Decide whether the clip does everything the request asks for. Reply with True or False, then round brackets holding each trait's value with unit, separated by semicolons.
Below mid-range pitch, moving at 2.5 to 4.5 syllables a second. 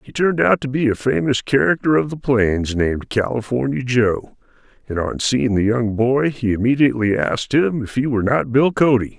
False (125 Hz; 5.3 syllables/s)